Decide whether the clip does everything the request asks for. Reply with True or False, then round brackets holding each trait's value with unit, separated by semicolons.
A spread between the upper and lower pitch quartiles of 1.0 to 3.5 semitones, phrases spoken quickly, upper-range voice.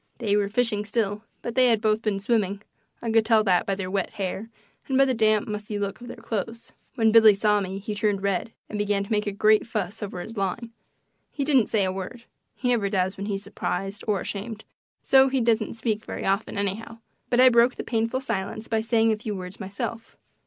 True (2.5 semitones; 225 wpm; 215 Hz)